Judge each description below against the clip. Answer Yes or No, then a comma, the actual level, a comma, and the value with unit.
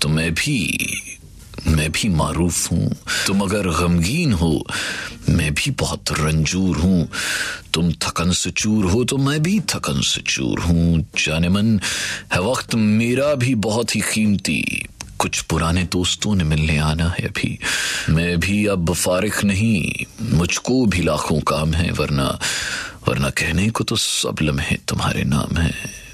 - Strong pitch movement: No, average, 4.8 semitones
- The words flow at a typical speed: Yes, average, 150 wpm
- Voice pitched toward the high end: No, very low, 90 Hz